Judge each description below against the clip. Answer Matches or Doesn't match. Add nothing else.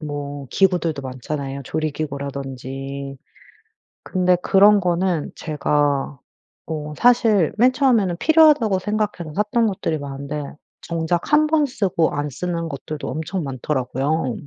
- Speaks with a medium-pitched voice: Matches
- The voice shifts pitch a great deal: Matches